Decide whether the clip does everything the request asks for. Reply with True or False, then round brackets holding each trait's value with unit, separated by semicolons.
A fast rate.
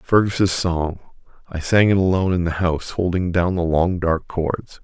False (185 wpm)